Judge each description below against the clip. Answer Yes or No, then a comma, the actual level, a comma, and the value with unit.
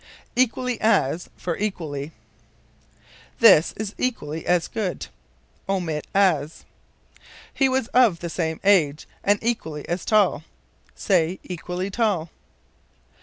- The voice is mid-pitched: Yes, medium, 180 Hz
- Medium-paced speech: No, slow, 110 wpm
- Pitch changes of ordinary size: Yes, average, 5.0 semitones